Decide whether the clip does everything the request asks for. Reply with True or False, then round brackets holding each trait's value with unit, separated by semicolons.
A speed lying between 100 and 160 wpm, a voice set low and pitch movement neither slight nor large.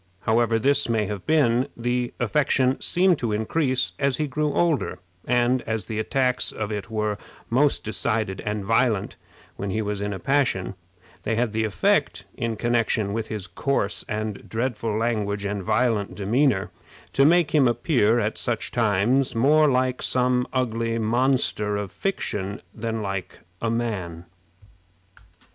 True (150 wpm; 115 Hz; 3.5 semitones)